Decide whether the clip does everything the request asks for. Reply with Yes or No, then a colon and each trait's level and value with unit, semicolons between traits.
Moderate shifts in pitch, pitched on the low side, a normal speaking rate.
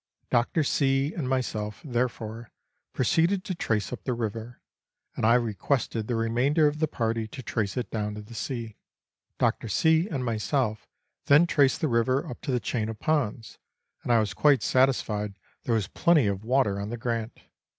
Yes: average, 3.9 semitones; low, 120 Hz; average, 180 wpm